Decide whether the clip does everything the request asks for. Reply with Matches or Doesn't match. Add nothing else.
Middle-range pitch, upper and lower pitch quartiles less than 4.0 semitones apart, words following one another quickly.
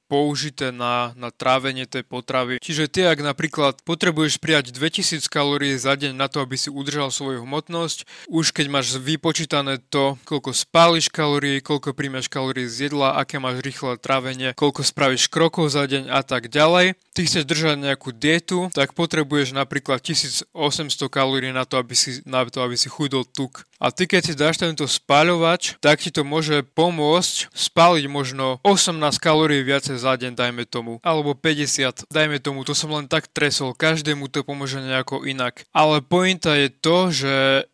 Matches